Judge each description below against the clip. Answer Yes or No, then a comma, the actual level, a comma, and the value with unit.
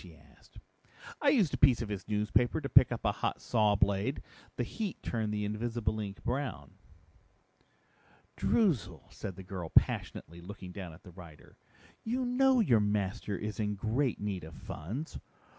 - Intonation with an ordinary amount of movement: Yes, average, 4.7 semitones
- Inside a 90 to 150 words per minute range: No, average, 165 wpm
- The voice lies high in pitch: No, low, 105 Hz